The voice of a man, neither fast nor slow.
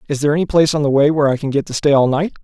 No: male; fast, 370 wpm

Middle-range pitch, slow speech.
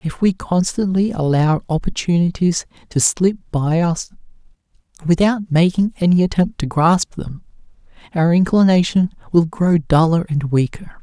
Yes: medium, 170 Hz; slow, 125 wpm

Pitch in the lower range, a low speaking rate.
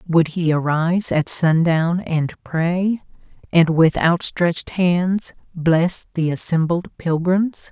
No: medium, 170 Hz; slow, 115 wpm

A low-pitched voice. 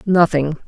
No: medium, 160 Hz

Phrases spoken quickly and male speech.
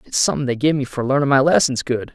Yes: fast, 280 wpm; male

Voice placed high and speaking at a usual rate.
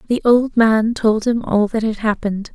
No: high, 220 Hz; fast, 210 wpm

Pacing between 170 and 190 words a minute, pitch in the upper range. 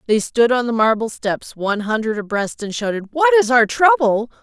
No: fast, 205 wpm; high, 215 Hz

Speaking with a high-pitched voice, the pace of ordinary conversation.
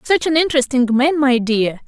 Yes: very high, 270 Hz; average, 190 wpm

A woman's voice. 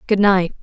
Yes: female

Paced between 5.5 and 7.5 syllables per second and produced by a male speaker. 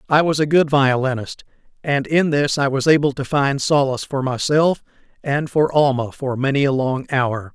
No: 4.9 syllables/s; male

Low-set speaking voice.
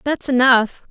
No: very high, 255 Hz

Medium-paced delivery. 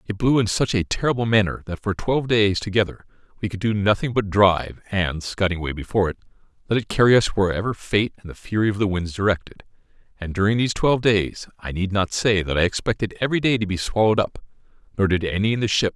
No: fast, 245 wpm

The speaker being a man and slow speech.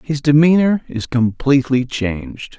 Yes: male; slow, 115 wpm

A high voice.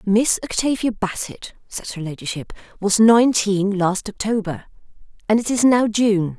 Yes: high, 205 Hz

